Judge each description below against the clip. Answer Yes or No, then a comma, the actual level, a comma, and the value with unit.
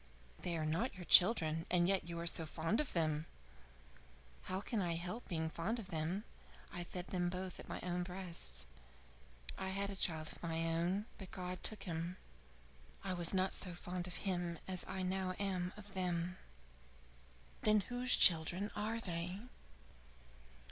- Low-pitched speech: No, medium, 180 Hz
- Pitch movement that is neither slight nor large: No, narrow, 2.3 semitones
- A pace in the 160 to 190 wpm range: Yes, average, 170 wpm